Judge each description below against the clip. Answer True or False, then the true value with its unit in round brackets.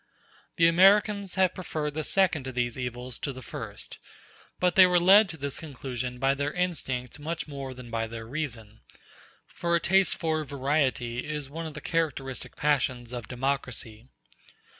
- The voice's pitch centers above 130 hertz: True (140 Hz)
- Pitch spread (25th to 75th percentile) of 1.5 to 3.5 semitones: False (4.8 semitones)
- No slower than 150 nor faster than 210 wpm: True (165 wpm)